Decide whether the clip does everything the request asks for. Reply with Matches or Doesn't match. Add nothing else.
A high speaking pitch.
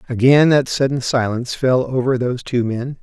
Doesn't match